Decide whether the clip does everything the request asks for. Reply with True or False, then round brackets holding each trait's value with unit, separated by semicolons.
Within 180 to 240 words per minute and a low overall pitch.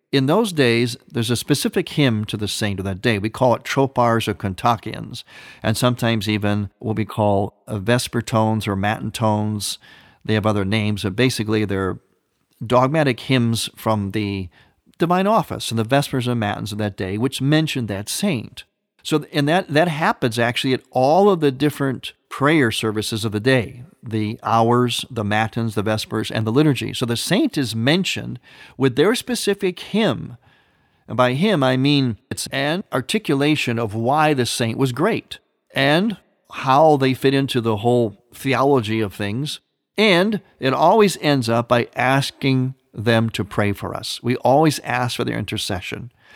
False (170 wpm; 120 Hz)